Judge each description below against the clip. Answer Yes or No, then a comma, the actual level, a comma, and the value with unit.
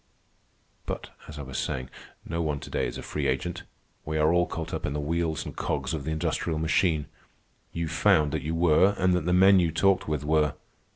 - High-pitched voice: No, very low, 80 Hz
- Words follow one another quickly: Yes, fast, 220 wpm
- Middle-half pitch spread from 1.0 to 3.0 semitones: Yes, narrow, 2.5 semitones